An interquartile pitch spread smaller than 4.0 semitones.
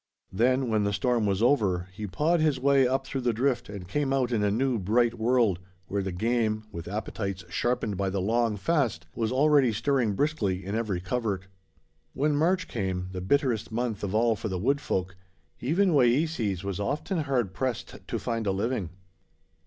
No: average, 5.1 semitones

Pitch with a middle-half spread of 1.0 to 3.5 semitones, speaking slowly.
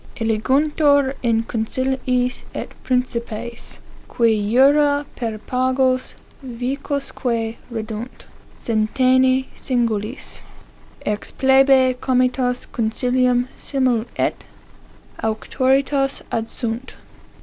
Yes: narrow, 2.6 semitones; slow, 75 wpm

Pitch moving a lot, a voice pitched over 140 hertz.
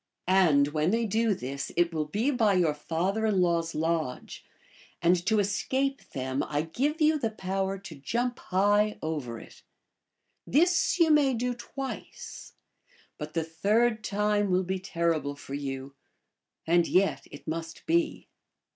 Yes: wide, 6.0 semitones; medium, 185 Hz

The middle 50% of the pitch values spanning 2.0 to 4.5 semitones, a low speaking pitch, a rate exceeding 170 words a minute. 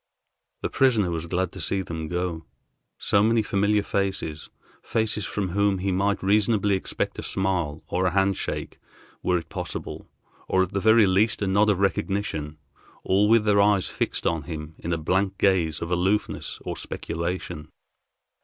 No: average, 2.9 semitones; very low, 95 Hz; average, 165 wpm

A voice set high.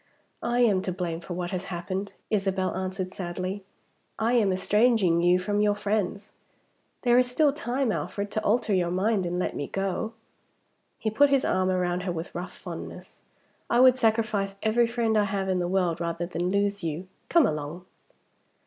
Yes: high, 195 Hz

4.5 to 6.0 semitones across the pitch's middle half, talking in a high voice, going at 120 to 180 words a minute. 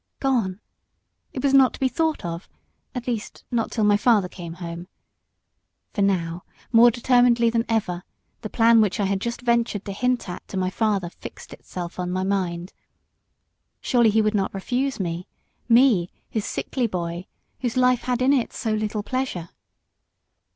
Yes: average, 4.9 semitones; high, 215 Hz; average, 170 wpm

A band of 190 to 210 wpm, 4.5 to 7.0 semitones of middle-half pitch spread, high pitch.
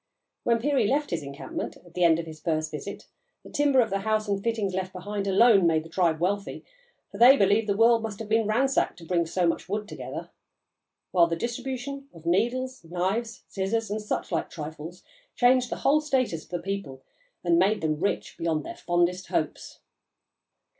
Yes: average, 195 wpm; average, 5.2 semitones; high, 195 Hz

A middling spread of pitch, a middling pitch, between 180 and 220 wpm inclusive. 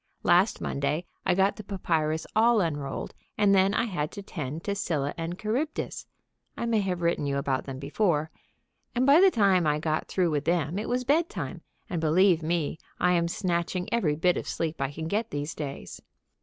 Yes: average, 4.7 semitones; medium, 175 Hz; average, 195 wpm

